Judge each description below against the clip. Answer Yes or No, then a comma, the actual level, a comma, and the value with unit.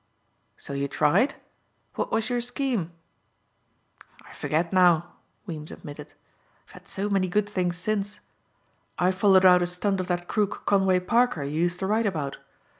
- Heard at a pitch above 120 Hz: Yes, medium, 185 Hz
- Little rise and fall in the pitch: No, average, 3.2 semitones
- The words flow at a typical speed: Yes, average, 160 wpm